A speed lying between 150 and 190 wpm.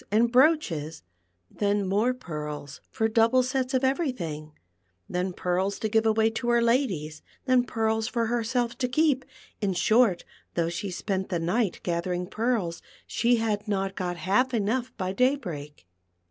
Yes: average, 160 wpm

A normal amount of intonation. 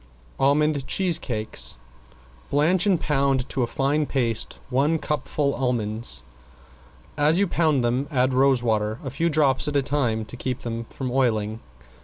Yes: average, 3.9 semitones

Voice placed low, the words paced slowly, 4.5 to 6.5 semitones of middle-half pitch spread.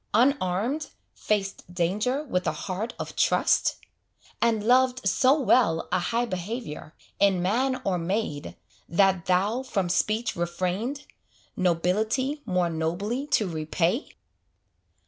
No: high, 200 Hz; slow, 115 wpm; wide, 5.5 semitones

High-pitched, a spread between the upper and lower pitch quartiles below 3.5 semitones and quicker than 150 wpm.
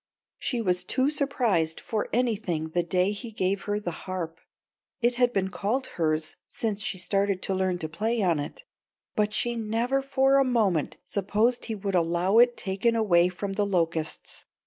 No: high, 200 Hz; average, 4.6 semitones; average, 175 wpm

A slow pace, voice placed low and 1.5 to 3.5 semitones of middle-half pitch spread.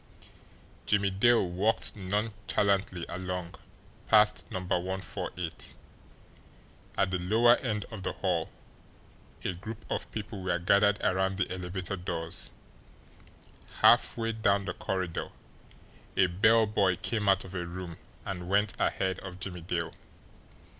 Yes: slow, 125 wpm; very low, 95 Hz; narrow, 2.4 semitones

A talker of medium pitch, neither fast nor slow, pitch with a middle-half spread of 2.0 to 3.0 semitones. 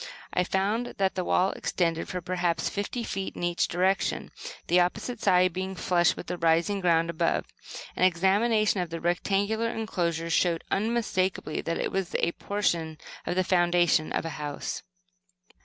Yes: medium, 180 Hz; average, 160 wpm; narrow, 2.5 semitones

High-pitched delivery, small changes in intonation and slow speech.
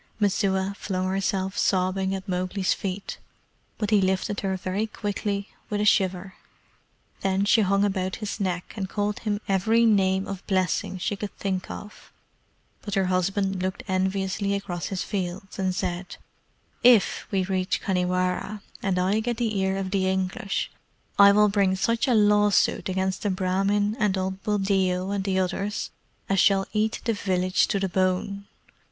No: high, 195 Hz; narrow, 1.5 semitones; average, 160 wpm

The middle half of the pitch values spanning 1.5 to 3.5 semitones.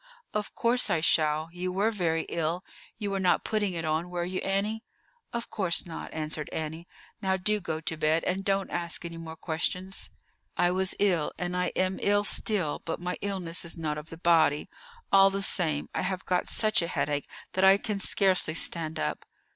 Yes: average, 3.2 semitones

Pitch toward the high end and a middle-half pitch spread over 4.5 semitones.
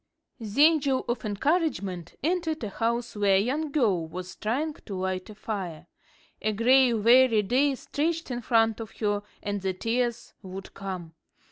Yes: high, 225 Hz; average, 5.1 semitones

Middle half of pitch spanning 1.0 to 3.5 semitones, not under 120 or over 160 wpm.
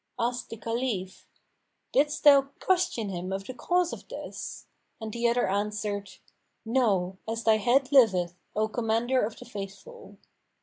No: average, 4.2 semitones; average, 145 wpm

